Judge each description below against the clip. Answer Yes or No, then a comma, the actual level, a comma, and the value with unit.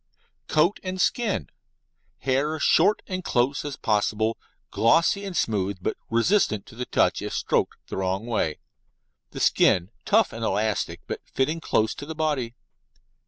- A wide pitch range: Yes, wide, 7.2 semitones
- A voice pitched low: Yes, low, 130 Hz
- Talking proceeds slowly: No, average, 150 wpm